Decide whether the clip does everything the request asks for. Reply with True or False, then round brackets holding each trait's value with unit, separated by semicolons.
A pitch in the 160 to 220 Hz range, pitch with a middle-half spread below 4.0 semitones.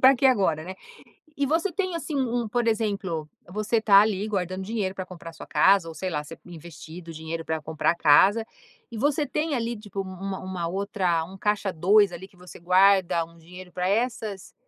False (190 Hz; 4.3 semitones)